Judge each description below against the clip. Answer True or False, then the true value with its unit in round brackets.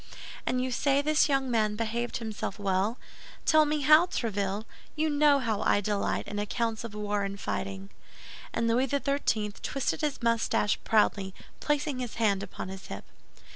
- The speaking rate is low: False (160 wpm)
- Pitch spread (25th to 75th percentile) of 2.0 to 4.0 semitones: False (5.1 semitones)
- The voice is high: True (230 Hz)